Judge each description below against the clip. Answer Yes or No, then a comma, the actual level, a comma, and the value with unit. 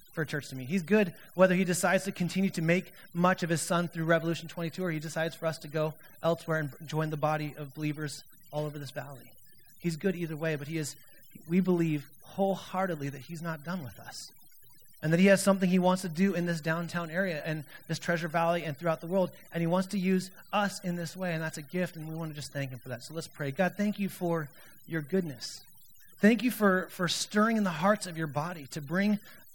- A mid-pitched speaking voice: Yes, medium, 170 Hz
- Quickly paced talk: Yes, fast, 245 wpm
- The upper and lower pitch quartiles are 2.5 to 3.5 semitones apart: Yes, average, 3.0 semitones